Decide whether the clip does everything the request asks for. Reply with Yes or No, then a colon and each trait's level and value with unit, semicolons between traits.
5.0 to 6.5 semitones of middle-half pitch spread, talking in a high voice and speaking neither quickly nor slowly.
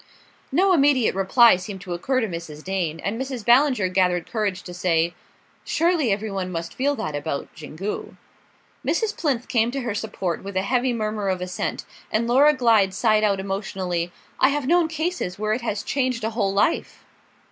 Yes: wide, 5.5 semitones; high, 215 Hz; average, 180 wpm